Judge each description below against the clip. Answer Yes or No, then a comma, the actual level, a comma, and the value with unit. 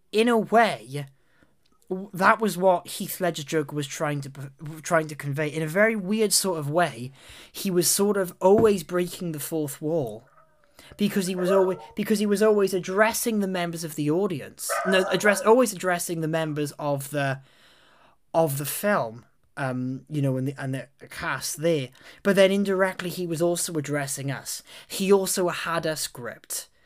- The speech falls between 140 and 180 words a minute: Yes, average, 175 wpm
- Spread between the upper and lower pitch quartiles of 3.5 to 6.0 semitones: Yes, average, 4.7 semitones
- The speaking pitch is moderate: Yes, medium, 175 Hz